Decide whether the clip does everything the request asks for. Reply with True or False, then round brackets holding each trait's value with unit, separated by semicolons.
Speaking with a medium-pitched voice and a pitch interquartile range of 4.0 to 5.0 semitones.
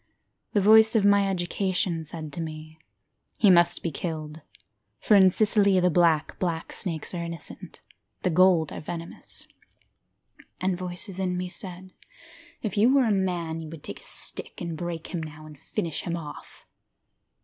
False (175 Hz; 2.8 semitones)